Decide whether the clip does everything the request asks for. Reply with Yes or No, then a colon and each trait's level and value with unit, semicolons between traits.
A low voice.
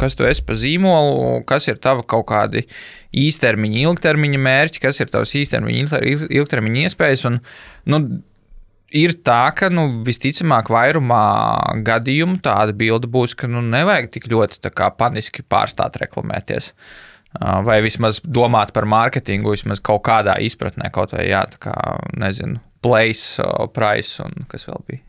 Yes: low, 120 Hz